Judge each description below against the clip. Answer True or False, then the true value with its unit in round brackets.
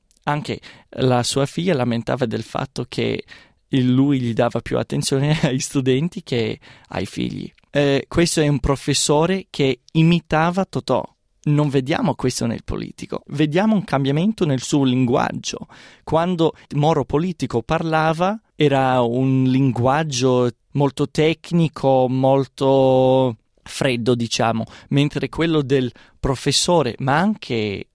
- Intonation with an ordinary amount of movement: True (3.5 semitones)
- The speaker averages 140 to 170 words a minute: False (120 wpm)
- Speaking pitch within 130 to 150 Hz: True (140 Hz)